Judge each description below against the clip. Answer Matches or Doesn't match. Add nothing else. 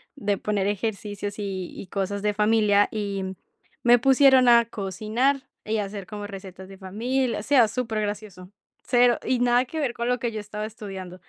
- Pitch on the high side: Matches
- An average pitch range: Matches